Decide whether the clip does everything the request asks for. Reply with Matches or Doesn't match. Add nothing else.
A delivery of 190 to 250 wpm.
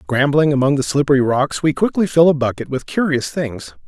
Matches